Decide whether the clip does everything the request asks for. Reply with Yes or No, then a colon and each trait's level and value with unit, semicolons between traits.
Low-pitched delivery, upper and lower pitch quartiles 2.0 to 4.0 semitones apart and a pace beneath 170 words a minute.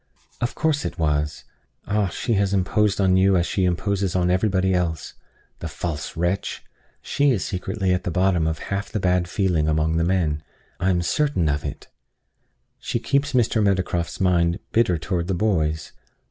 No: very low, 90 Hz; average, 2.9 semitones; average, 175 wpm